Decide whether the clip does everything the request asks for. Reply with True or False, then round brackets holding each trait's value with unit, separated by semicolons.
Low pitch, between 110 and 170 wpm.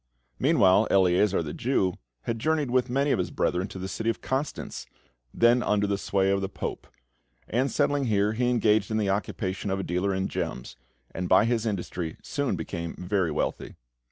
False (100 Hz; 185 wpm)